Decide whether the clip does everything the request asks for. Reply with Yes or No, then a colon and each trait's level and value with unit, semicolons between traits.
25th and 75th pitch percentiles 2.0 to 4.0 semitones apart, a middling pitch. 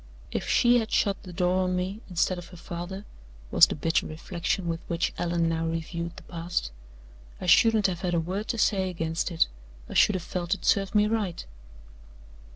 Yes: narrow, 2.6 semitones; medium, 180 Hz